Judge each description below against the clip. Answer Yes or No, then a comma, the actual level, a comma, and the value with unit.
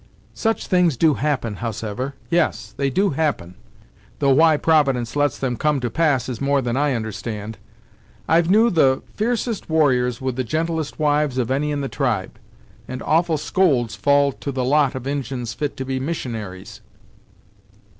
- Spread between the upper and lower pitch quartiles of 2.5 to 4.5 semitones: Yes, average, 3.9 semitones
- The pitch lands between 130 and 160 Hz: Yes, medium, 140 Hz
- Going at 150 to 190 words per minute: Yes, average, 165 wpm